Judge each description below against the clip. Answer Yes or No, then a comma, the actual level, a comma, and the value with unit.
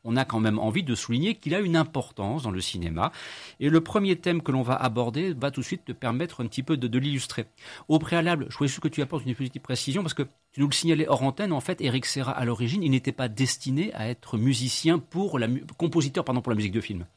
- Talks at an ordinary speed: No, fast, 265 wpm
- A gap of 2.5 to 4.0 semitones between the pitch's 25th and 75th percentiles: No, average, 4.8 semitones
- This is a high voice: No, low, 135 Hz